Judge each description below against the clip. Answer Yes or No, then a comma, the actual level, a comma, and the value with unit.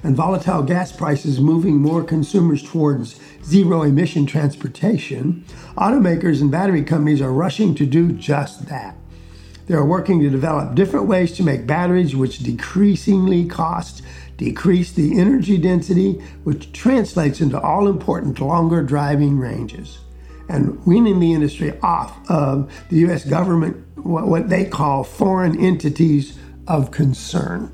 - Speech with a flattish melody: No, average, 4.0 semitones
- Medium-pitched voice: Yes, medium, 160 Hz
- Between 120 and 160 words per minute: Yes, slow, 135 wpm